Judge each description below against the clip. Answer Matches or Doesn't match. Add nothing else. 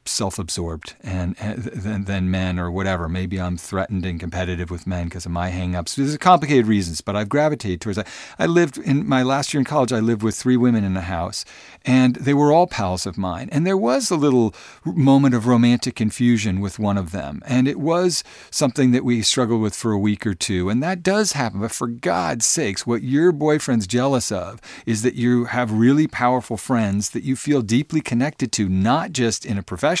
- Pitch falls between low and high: Doesn't match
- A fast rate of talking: Matches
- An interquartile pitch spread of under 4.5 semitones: Doesn't match